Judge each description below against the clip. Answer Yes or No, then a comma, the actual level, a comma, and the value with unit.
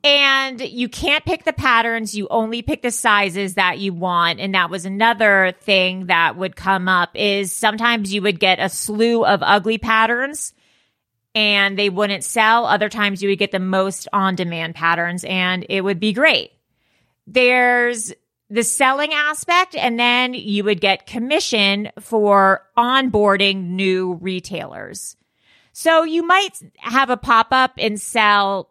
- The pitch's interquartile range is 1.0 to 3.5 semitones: No, average, 4.0 semitones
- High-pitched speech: Yes, high, 210 Hz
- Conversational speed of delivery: Yes, average, 155 wpm